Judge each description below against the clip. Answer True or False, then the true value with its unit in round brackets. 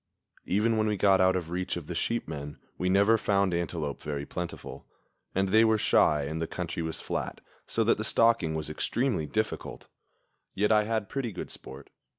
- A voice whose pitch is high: False (95 Hz)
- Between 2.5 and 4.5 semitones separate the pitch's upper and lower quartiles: False (5.0 semitones)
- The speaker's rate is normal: True (190 wpm)